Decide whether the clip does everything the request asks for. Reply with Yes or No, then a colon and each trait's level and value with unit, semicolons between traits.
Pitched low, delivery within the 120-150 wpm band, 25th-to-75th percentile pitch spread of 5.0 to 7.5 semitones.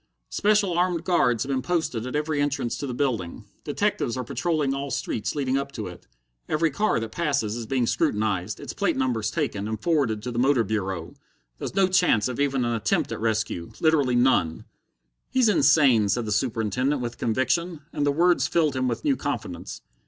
No: low, 130 Hz; average, 190 wpm; wide, 5.6 semitones